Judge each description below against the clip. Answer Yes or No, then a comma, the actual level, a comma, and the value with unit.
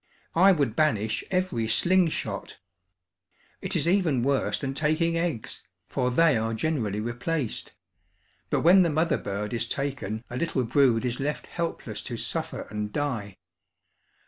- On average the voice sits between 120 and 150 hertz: Yes, medium, 140 Hz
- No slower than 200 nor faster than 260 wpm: No, average, 145 wpm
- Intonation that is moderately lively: No, wide, 6.6 semitones